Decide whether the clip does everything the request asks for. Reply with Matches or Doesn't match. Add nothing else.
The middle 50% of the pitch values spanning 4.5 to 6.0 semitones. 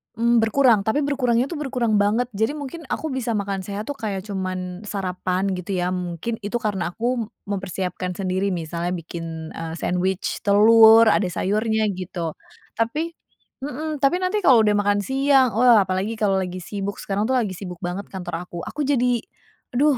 Matches